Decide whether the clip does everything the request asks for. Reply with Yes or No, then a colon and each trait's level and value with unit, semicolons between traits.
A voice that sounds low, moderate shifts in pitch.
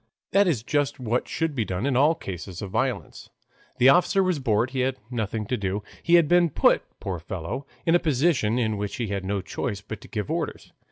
No: low, 120 Hz; wide, 6.1 semitones